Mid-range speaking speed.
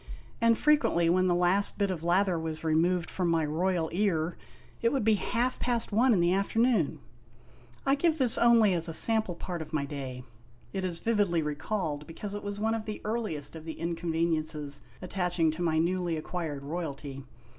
Yes: average, 190 wpm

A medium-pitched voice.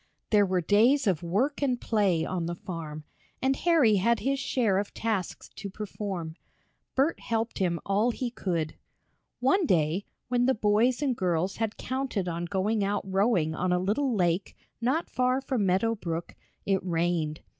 No: high, 205 Hz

